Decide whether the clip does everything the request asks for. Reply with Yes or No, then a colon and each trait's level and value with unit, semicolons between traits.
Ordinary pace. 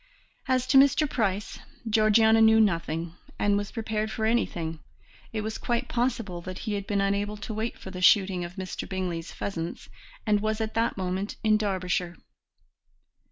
Yes: average, 165 wpm